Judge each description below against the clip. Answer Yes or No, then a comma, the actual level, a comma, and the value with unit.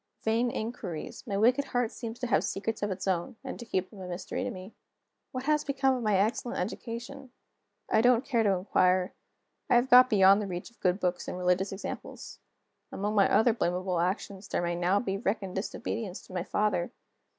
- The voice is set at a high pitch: Yes, high, 205 Hz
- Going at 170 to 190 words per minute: No, average, 200 wpm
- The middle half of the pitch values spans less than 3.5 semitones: No, average, 4.4 semitones